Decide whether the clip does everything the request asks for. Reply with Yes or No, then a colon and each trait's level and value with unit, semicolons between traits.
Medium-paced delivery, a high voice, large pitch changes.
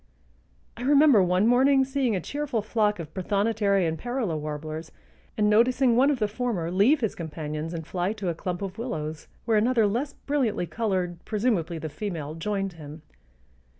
Yes: average, 170 wpm; high, 205 Hz; wide, 6.3 semitones